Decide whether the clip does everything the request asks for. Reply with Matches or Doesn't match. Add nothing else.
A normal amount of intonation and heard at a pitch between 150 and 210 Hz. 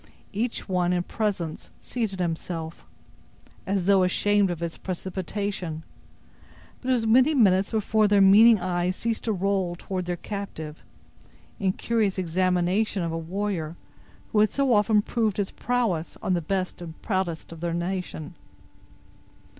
Matches